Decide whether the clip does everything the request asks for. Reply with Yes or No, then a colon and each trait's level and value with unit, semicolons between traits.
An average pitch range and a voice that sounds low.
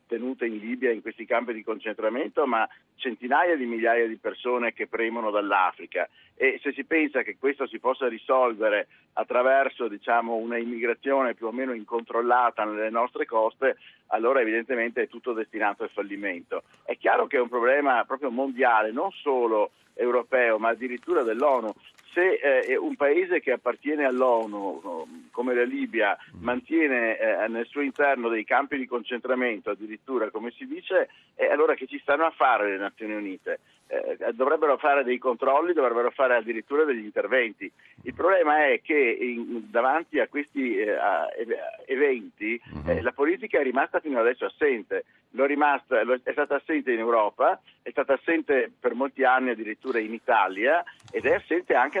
No: wide, 6.0 semitones; low, 130 Hz